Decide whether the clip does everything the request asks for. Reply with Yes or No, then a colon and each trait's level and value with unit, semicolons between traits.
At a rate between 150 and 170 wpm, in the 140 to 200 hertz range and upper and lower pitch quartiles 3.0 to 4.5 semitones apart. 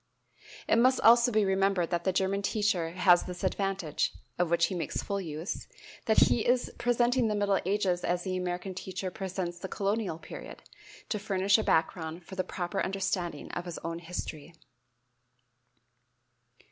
No: average, 160 wpm; high, 190 Hz; narrow, 2.6 semitones